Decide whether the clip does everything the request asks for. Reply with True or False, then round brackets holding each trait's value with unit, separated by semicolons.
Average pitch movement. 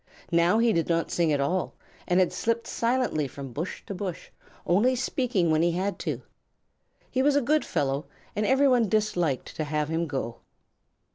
False (6.8 semitones)